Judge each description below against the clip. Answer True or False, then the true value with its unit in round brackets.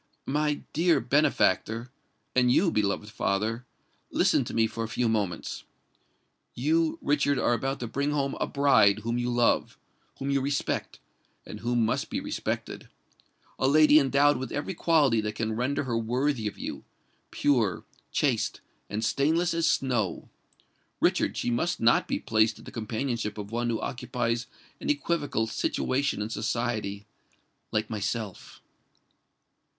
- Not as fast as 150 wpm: True (135 wpm)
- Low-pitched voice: True (120 Hz)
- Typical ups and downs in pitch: True (4.1 semitones)